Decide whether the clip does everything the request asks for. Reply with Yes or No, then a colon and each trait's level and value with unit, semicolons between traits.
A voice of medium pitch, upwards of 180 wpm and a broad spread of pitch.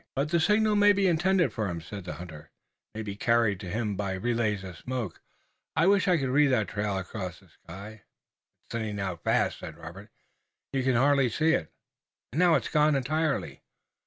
No: low, 115 Hz; average, 200 wpm; wide, 7.6 semitones